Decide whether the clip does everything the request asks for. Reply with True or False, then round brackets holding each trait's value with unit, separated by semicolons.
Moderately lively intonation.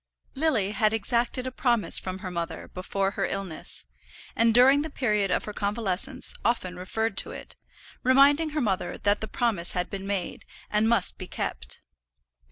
True (4.6 semitones)